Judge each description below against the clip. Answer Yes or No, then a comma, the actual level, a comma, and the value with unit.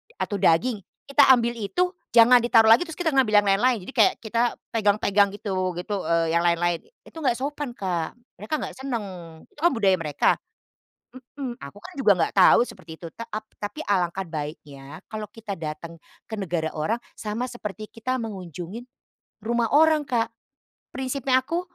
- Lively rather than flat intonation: Yes, wide, 5.8 semitones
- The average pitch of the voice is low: No, high, 215 Hz